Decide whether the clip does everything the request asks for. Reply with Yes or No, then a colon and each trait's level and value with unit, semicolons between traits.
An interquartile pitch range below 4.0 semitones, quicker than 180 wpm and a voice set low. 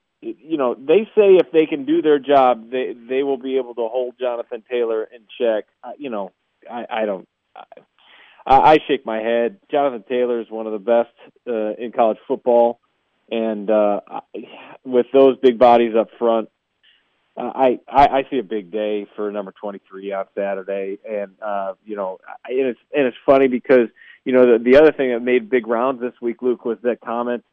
Yes: average, 3.1 semitones; average, 200 wpm; low, 120 Hz